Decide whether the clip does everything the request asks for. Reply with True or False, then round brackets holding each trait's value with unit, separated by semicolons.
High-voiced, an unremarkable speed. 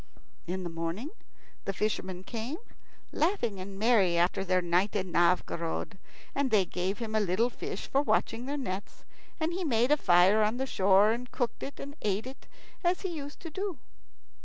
True (215 Hz; 185 wpm)